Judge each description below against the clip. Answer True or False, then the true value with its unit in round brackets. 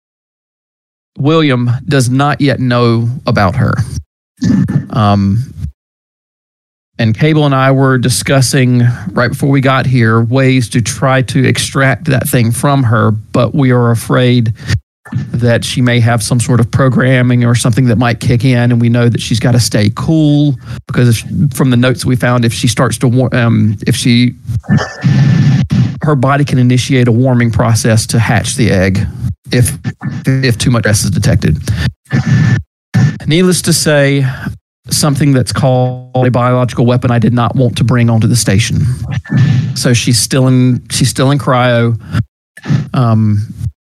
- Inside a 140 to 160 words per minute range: True (155 wpm)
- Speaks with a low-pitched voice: True (125 Hz)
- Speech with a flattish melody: True (2.3 semitones)